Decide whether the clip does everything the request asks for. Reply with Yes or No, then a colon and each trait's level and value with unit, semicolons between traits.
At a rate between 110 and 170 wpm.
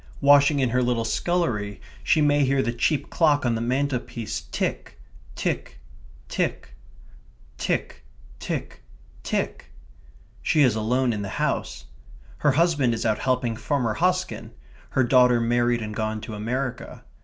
Yes: average, 140 wpm